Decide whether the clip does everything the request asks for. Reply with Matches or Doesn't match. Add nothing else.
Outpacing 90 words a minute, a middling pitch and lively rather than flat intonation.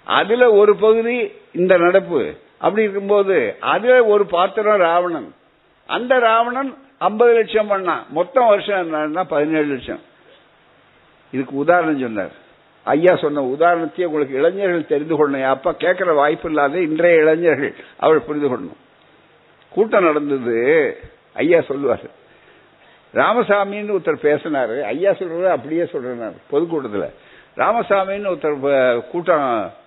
Matches